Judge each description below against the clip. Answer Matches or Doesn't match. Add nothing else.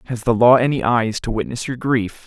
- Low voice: Matches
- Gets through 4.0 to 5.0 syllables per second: Doesn't match